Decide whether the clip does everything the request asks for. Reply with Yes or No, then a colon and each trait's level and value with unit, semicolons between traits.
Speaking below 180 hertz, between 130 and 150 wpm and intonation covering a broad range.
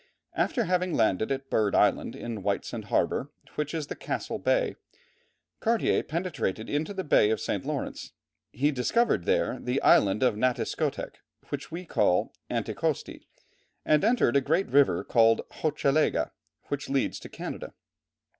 Yes: medium, 140 Hz; average, 145 wpm; wide, 6.5 semitones